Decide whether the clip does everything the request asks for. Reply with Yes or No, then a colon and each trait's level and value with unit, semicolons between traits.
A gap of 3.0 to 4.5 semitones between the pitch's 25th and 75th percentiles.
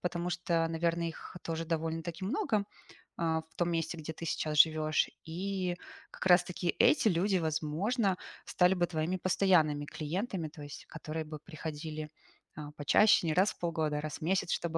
No: narrow, 2.4 semitones